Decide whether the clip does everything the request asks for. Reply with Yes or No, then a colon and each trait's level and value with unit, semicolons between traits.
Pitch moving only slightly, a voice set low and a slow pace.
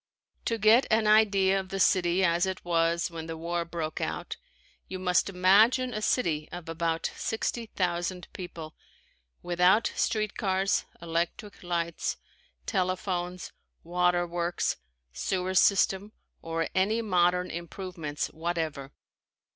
No: narrow, 2.3 semitones; medium, 180 Hz; slow, 120 wpm